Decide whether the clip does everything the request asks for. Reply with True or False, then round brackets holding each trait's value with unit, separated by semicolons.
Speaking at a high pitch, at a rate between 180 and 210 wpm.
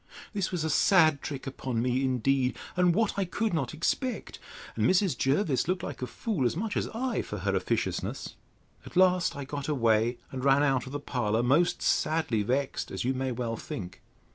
False (140 Hz; 190 wpm)